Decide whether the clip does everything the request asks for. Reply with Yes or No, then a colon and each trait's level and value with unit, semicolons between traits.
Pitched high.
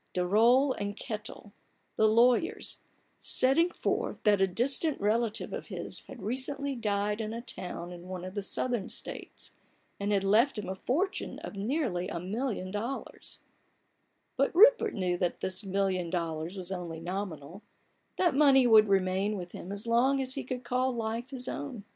Yes: high, 215 Hz